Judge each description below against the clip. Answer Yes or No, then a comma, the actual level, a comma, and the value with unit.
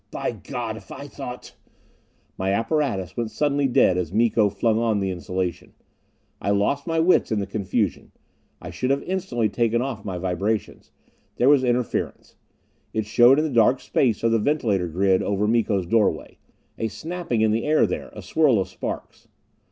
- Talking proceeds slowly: No, average, 175 wpm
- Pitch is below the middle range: Yes, low, 110 Hz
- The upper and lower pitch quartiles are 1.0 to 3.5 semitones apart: No, average, 4.7 semitones